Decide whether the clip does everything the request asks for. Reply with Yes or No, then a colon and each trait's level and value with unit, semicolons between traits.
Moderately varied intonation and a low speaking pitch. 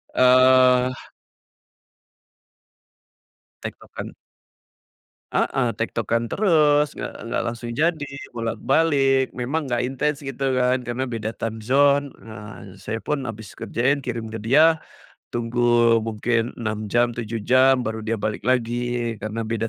Yes: average, 3.0 semitones; low, 120 Hz